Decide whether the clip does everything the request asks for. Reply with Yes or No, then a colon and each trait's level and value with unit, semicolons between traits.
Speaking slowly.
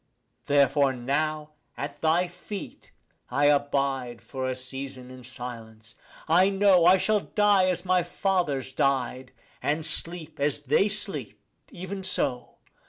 Yes: slow, 130 wpm